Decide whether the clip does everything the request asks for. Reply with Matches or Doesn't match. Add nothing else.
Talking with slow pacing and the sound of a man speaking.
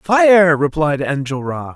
Matches